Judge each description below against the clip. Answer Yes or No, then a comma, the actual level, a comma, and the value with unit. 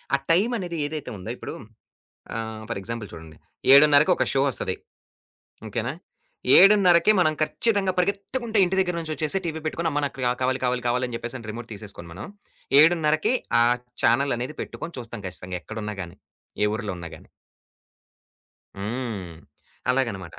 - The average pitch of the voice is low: Yes, low, 130 Hz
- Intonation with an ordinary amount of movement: No, wide, 7.3 semitones